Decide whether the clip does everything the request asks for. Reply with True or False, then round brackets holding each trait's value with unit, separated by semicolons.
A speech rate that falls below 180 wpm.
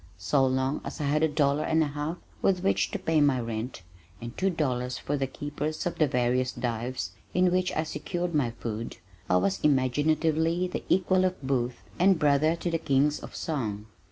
False (195 wpm)